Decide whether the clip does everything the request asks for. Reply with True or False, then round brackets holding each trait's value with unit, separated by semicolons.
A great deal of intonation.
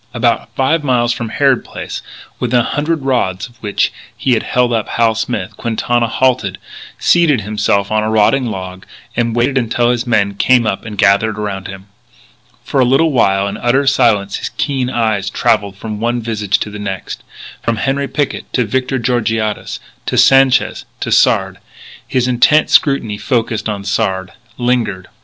False (3.6 semitones)